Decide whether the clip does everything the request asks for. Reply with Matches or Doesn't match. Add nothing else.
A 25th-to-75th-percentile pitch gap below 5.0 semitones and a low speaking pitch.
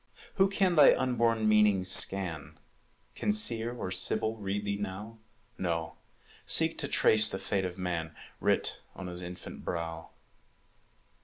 Matches